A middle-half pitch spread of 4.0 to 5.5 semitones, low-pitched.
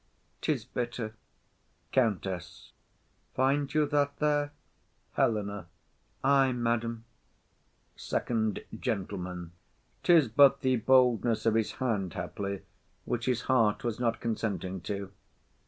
Yes: average, 4.4 semitones; low, 115 Hz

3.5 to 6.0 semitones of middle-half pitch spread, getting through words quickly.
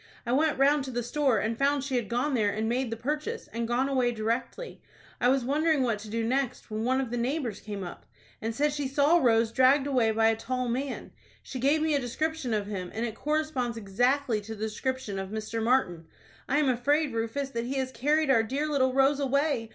Yes: average, 3.8 semitones; fast, 230 wpm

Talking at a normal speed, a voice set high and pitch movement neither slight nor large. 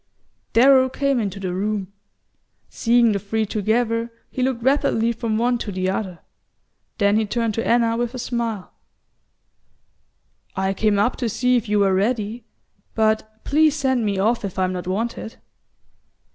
Yes: average, 160 wpm; high, 225 Hz; average, 3.1 semitones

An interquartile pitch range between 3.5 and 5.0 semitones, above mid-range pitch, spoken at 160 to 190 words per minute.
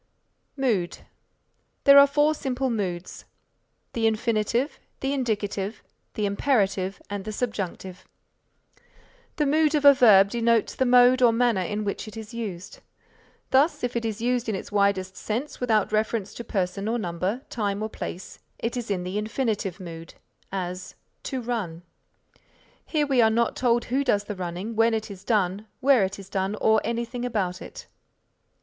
Yes: average, 3.9 semitones; high, 220 Hz; average, 165 wpm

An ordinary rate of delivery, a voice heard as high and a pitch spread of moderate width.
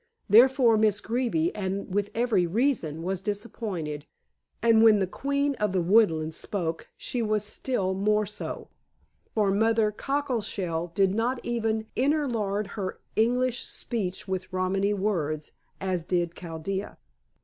No: slow, 130 wpm; high, 205 Hz; average, 3.7 semitones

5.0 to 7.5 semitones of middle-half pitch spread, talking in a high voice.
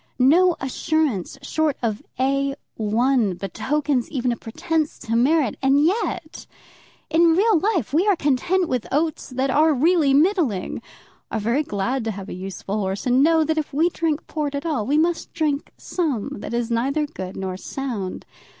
Yes: average, 5.3 semitones; very high, 275 Hz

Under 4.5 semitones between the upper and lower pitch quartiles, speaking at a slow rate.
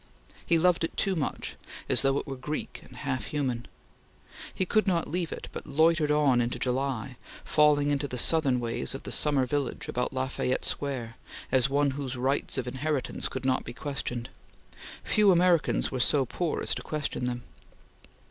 No: average, 3.2 semitones; average, 180 wpm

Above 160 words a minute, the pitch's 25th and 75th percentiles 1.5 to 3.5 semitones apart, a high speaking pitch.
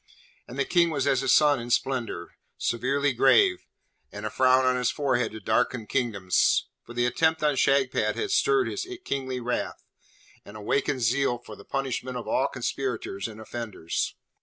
No: average, 170 wpm; average, 3.0 semitones; low, 130 Hz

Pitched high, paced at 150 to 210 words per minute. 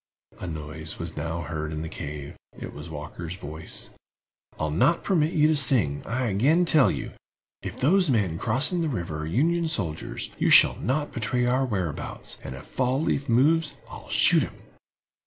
No: low, 110 Hz; average, 175 wpm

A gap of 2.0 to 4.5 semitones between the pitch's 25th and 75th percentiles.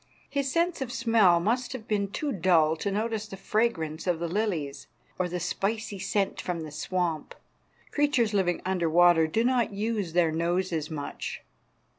No: average, 5.0 semitones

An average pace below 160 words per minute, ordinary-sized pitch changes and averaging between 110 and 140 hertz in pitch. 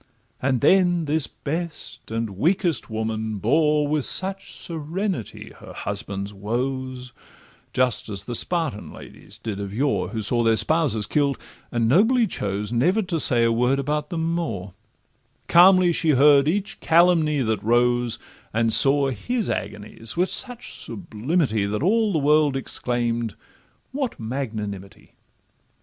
No: slow, 135 wpm; wide, 6.7 semitones; low, 135 Hz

